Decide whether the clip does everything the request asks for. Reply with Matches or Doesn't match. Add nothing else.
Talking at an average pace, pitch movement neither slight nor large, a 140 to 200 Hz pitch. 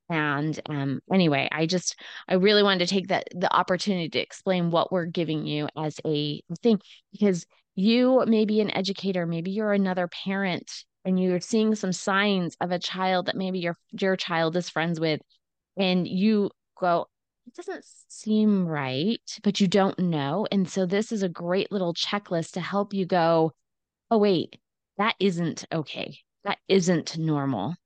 Matches